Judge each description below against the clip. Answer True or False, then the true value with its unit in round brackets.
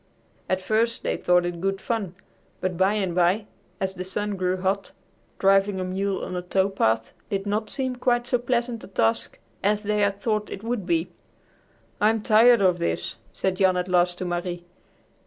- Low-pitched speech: False (195 Hz)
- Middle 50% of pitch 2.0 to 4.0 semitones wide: True (2.8 semitones)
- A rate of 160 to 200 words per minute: True (190 wpm)